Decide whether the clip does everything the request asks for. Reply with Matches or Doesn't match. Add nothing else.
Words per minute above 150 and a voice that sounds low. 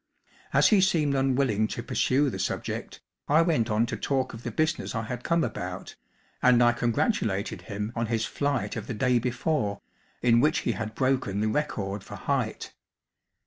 Matches